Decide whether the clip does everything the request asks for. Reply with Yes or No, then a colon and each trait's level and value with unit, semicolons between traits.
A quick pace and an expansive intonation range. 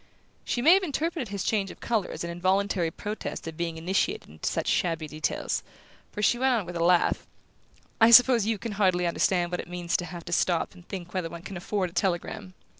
No: fast, 220 wpm; average, 4.0 semitones